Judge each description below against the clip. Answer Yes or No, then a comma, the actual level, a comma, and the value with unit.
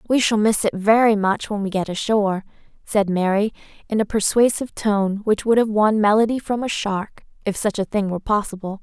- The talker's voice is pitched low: No, high, 210 Hz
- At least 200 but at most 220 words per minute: Yes, fast, 205 wpm